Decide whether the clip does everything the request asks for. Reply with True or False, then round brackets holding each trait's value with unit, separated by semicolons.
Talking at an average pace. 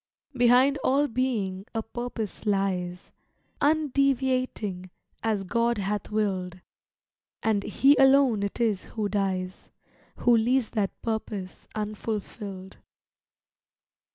False (100 wpm)